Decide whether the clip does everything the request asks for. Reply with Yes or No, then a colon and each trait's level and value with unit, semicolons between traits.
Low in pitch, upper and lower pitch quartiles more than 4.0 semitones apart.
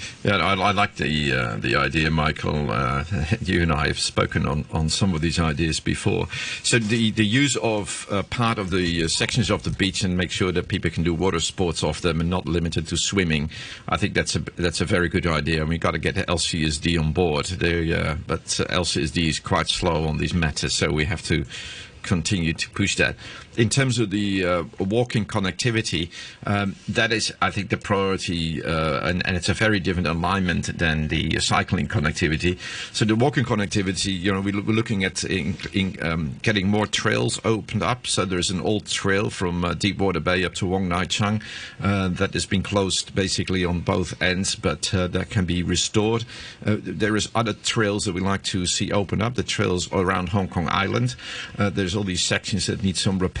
No: very low, 95 Hz; average, 3.2 semitones